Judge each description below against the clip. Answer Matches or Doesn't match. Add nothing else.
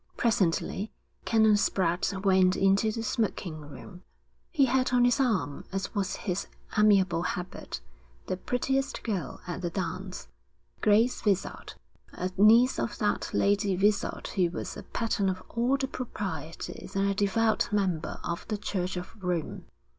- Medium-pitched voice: Doesn't match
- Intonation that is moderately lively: Matches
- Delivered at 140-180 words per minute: Matches